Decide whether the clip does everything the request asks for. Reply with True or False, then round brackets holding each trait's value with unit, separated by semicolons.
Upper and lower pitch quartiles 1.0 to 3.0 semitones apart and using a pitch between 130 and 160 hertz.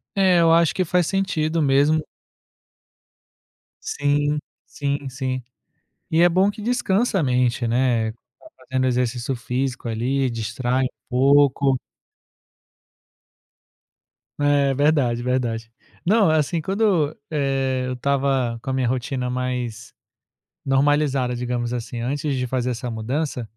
False (3.4 semitones; 135 Hz)